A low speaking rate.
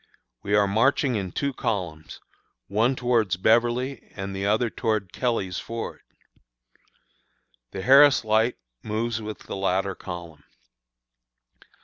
Yes: slow, 115 wpm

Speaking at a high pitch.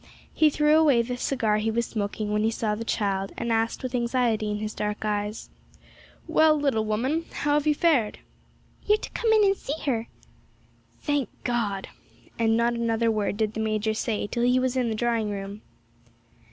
Yes: high, 230 Hz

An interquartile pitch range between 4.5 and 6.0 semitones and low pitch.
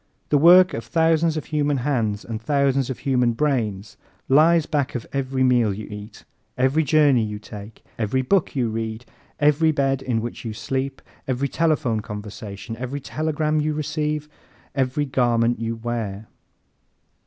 Yes: average, 4.8 semitones; low, 130 Hz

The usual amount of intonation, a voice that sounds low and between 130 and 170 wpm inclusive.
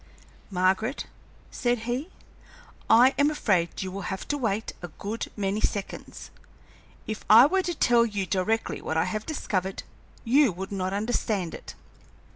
No: average, 4.2 semitones; high, 215 Hz; average, 150 wpm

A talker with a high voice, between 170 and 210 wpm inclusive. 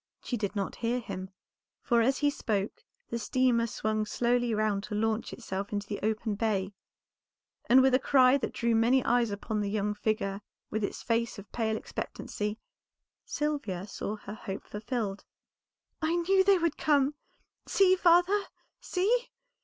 No: high, 230 Hz; average, 160 wpm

